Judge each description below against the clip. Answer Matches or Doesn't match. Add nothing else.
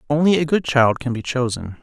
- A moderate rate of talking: Doesn't match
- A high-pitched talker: Doesn't match